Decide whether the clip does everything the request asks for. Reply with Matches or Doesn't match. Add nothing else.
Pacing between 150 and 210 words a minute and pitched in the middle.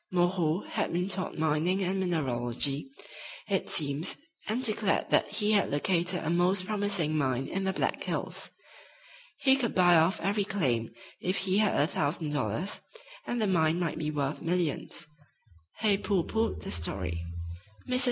Matches